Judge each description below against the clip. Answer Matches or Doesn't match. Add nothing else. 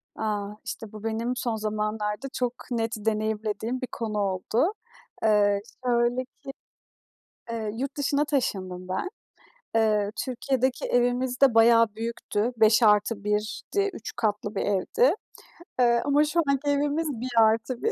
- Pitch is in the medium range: Doesn't match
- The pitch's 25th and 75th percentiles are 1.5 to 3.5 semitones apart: Matches